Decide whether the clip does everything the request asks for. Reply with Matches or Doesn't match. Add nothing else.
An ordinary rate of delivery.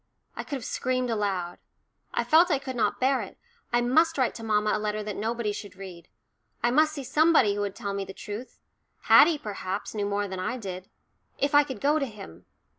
Doesn't match